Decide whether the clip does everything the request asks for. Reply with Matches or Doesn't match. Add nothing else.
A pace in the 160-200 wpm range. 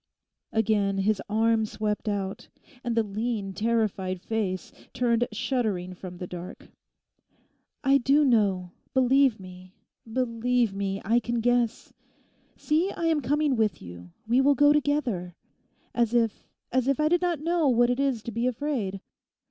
Doesn't match